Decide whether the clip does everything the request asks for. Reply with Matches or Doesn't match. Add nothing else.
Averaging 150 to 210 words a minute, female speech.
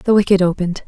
Matches